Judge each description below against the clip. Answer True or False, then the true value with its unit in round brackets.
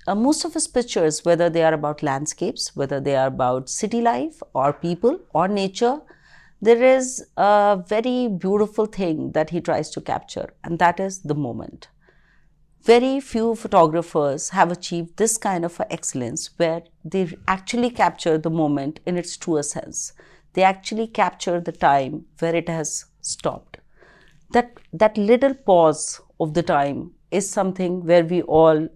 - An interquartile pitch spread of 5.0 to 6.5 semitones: True (5.3 semitones)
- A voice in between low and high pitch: True (175 Hz)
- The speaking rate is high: False (160 wpm)